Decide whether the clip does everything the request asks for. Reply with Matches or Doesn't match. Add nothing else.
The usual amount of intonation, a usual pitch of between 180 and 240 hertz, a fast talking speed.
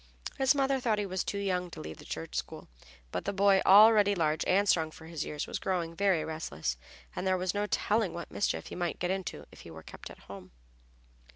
Matches